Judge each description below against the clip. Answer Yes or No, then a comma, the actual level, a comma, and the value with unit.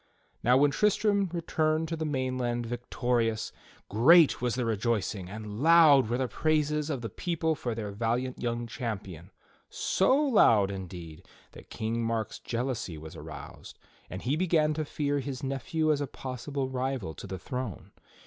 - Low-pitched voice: Yes, low, 125 Hz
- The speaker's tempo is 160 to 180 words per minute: Yes, average, 165 wpm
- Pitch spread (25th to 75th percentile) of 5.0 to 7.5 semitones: Yes, wide, 5.5 semitones